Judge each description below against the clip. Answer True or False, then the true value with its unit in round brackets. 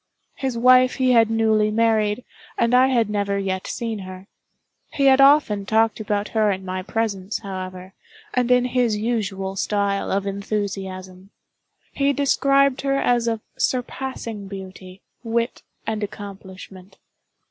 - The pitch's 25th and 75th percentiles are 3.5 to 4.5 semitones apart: True (3.9 semitones)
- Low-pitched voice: False (215 Hz)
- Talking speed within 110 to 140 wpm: True (135 wpm)